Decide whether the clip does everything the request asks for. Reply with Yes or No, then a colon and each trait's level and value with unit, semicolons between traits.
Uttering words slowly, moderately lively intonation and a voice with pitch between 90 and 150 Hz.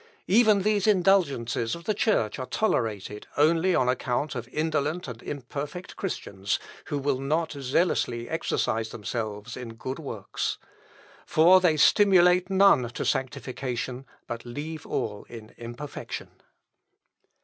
No: slow, 125 wpm; wide, 6.8 semitones; medium, 140 Hz